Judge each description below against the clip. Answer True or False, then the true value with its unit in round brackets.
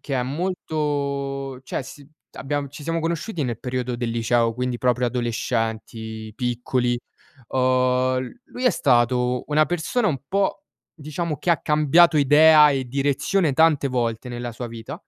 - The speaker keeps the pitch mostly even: False (3.8 semitones)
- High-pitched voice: False (135 Hz)